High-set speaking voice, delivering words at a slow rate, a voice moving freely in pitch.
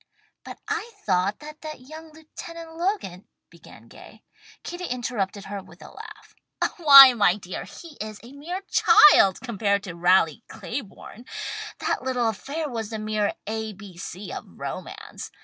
No: high, 230 Hz; average, 150 wpm; wide, 7.2 semitones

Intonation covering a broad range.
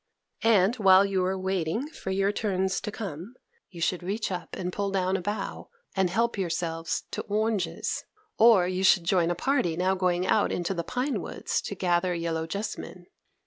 No: narrow, 2.4 semitones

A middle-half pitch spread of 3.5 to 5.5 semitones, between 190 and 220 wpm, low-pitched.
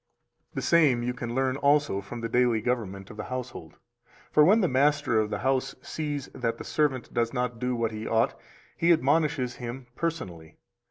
Yes: average, 4.0 semitones; average, 195 wpm; low, 125 Hz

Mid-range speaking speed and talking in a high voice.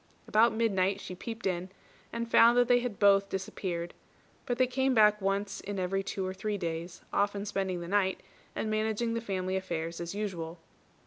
Yes: average, 185 wpm; high, 200 Hz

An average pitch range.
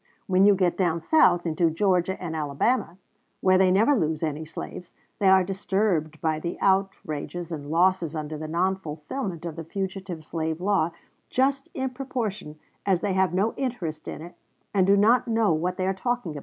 Yes: average, 3.7 semitones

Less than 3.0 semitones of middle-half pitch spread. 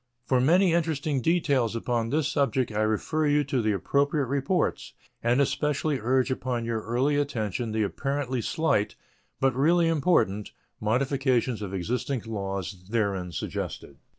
No: average, 4.7 semitones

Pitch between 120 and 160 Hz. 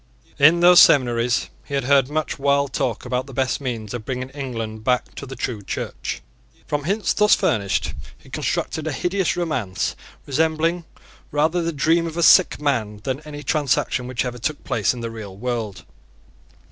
Yes: low, 135 Hz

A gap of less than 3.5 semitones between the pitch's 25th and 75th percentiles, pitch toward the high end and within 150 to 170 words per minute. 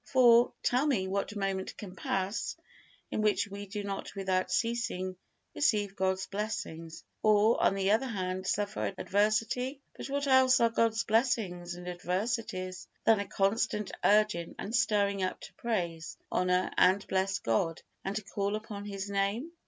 Yes: average, 2.9 semitones; high, 200 Hz; average, 155 wpm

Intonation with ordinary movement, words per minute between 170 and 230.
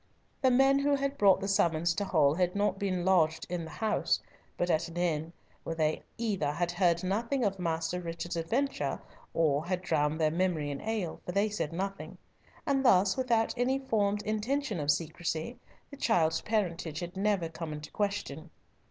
Yes: average, 4.5 semitones; average, 180 wpm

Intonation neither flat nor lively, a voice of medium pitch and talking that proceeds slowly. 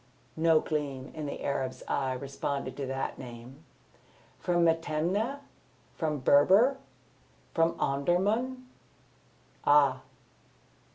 Yes: average, 4.2 semitones; medium, 150 Hz; slow, 95 wpm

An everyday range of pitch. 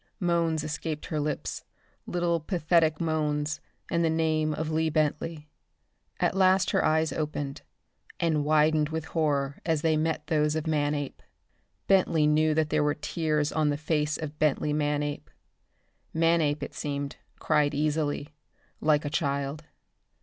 No: narrow, 1.3 semitones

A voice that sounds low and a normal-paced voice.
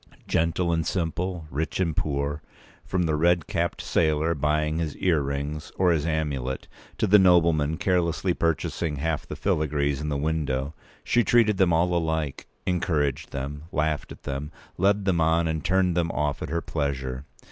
Yes: very low, 80 Hz; average, 160 wpm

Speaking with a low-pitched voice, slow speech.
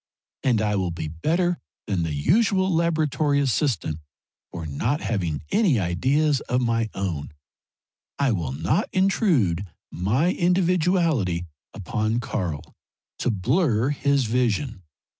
Yes: low, 120 Hz; slow, 120 wpm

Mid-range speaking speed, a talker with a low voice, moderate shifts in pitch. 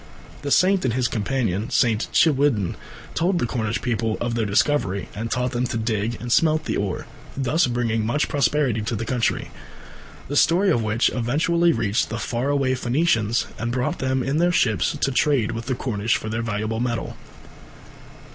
Yes: average, 180 wpm; low, 120 Hz; average, 3.8 semitones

